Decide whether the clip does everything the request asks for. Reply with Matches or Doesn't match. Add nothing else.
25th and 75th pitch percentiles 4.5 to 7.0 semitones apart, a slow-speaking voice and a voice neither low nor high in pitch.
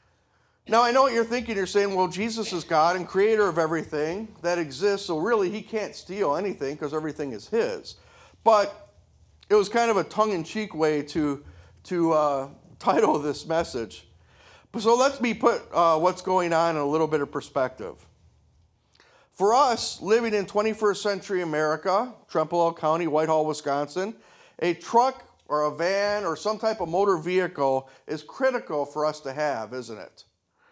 Doesn't match